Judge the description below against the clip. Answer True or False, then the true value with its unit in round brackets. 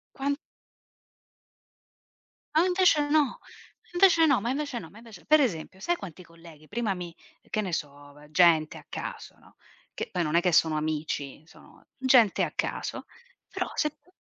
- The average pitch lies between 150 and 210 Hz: True (190 Hz)